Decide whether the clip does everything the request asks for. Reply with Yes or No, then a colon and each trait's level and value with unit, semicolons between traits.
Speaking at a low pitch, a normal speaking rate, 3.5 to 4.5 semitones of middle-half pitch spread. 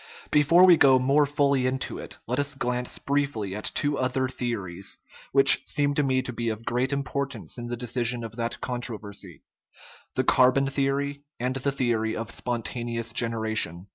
No: low, 125 Hz; average, 170 wpm; average, 3.1 semitones